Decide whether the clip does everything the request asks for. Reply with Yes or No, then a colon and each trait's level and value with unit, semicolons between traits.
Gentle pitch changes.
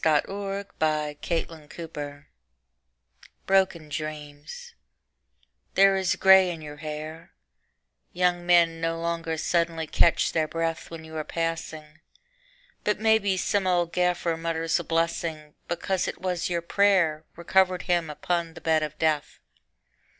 Yes: narrow, 2.3 semitones